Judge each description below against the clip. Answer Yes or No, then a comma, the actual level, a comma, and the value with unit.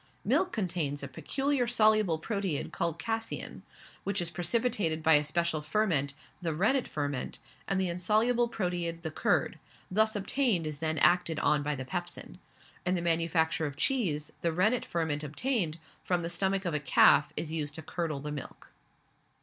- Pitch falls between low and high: Yes, medium, 170 Hz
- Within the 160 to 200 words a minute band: Yes, average, 165 wpm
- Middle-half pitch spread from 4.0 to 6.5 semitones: Yes, average, 5.0 semitones